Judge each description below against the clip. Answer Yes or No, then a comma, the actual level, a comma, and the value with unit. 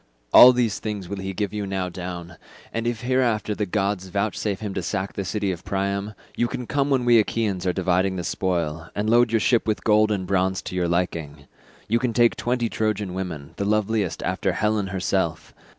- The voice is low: Yes, low, 100 Hz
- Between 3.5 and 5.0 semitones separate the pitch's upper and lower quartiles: No, average, 3.1 semitones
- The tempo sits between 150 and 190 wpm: No, fast, 205 wpm